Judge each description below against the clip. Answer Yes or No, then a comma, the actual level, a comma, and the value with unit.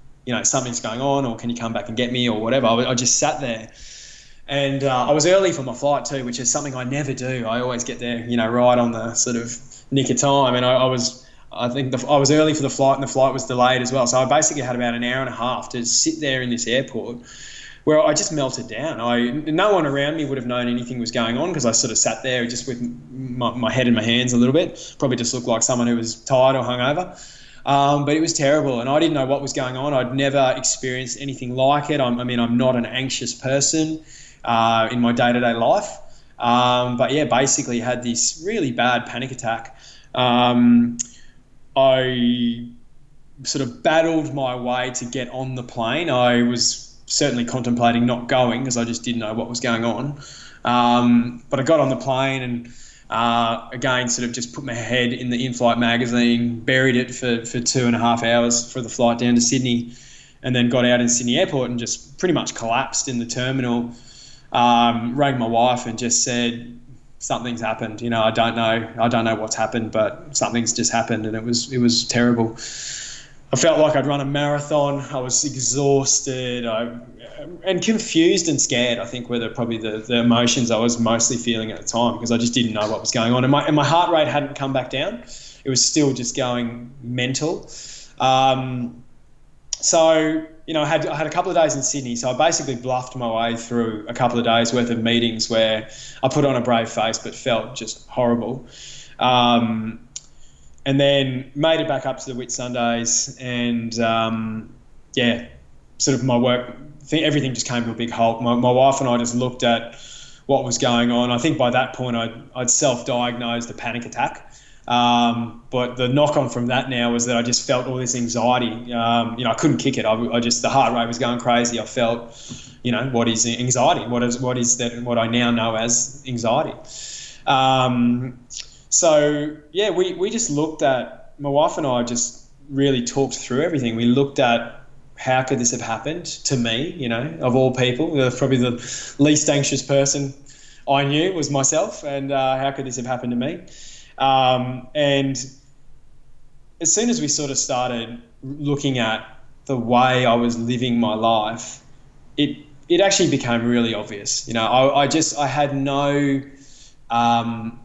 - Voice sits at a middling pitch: No, low, 125 Hz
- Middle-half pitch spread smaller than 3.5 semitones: Yes, narrow, 2.4 semitones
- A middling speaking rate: No, fast, 210 wpm